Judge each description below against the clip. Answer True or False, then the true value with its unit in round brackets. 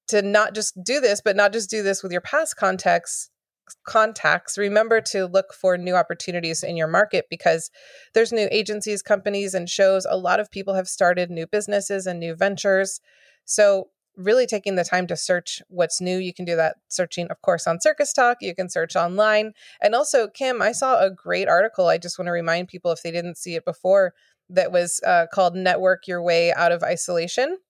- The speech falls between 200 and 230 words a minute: True (205 wpm)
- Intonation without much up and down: False (3.2 semitones)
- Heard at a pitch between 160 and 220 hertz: True (190 Hz)